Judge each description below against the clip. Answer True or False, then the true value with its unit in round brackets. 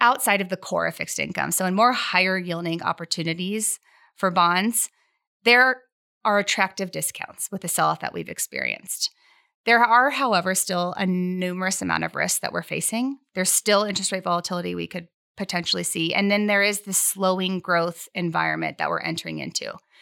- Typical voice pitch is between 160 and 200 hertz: True (190 Hz)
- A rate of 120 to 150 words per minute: False (175 wpm)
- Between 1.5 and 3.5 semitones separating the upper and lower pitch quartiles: False (4.5 semitones)